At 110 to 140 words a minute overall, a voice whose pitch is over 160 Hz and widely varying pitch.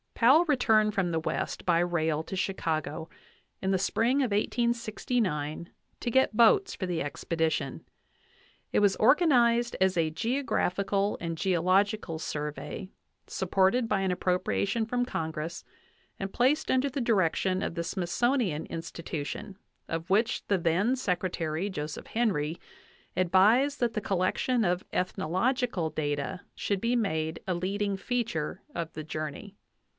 Yes: slow, 135 wpm; high, 190 Hz; wide, 5.8 semitones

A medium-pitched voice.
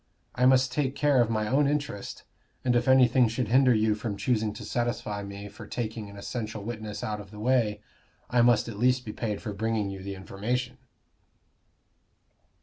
No: low, 115 Hz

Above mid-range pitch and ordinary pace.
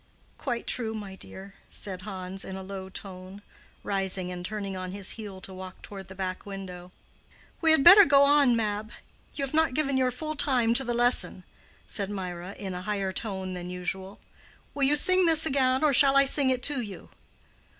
Yes: high, 205 Hz; average, 195 wpm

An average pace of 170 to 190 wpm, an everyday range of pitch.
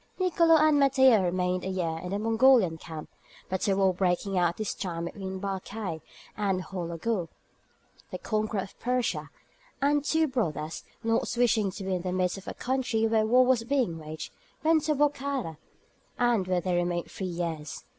No: average, 175 wpm; wide, 5.9 semitones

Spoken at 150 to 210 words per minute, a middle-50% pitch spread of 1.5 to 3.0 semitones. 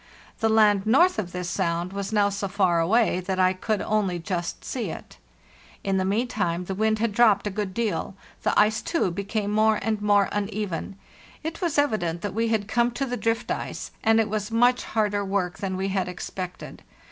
Yes: average, 200 wpm; average, 2.7 semitones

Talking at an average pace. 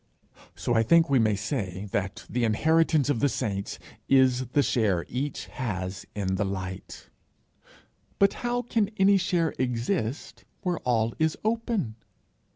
Yes: average, 145 wpm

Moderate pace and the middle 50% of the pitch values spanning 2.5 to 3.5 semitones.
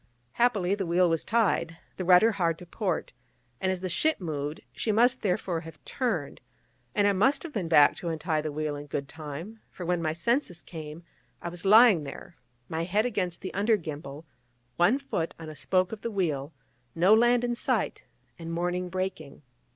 No: average, 190 wpm; average, 4.5 semitones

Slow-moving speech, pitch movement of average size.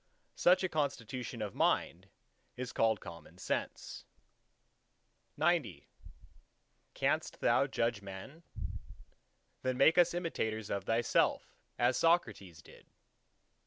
No: slow, 105 wpm; wide, 7.5 semitones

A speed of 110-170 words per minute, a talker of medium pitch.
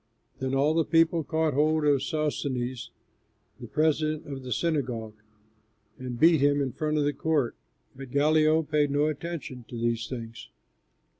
Yes: average, 155 wpm; medium, 145 Hz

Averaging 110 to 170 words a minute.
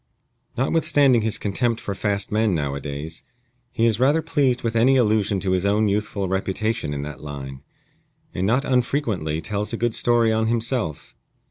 Yes: average, 160 wpm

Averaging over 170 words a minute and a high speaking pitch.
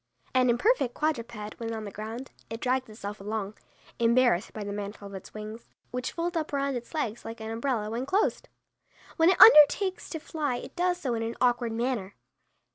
Yes: average, 195 wpm; high, 235 Hz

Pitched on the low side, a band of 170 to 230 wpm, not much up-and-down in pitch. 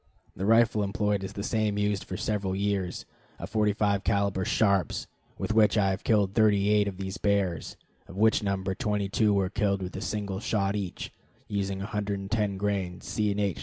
Yes: low, 100 Hz; average, 185 wpm; narrow, 1.3 semitones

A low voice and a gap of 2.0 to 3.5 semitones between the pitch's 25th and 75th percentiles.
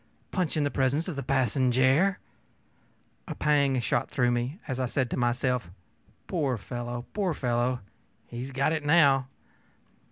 Yes: low, 130 Hz; average, 3.1 semitones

